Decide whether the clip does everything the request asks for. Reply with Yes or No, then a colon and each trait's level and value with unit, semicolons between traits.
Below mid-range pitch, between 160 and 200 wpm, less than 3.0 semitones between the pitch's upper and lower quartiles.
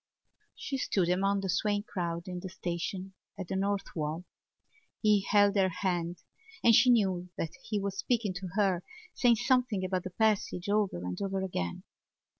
No: high, 190 Hz; average, 170 wpm; narrow, 2.5 semitones